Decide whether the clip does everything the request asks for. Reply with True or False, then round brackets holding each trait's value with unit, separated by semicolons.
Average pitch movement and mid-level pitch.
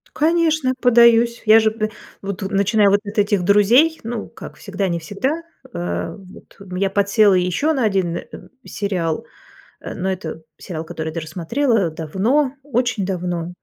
False (4.7 semitones; 200 Hz)